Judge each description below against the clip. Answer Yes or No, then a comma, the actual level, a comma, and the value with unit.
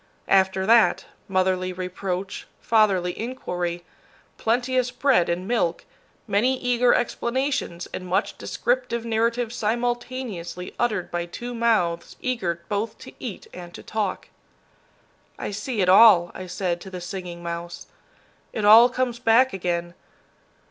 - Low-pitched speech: No, high, 205 Hz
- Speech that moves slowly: Yes, slow, 130 wpm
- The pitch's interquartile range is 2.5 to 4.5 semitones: No, average, 5.1 semitones